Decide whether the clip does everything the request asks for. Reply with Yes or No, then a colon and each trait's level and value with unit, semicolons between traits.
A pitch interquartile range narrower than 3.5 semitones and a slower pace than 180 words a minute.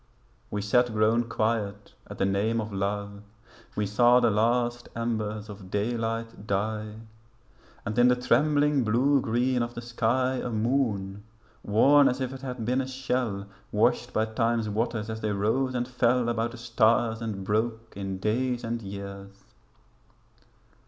Yes: average, 2.7 semitones; average, 155 wpm